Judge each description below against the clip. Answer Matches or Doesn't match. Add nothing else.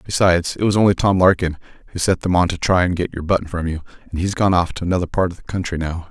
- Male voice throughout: Matches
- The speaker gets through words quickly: Matches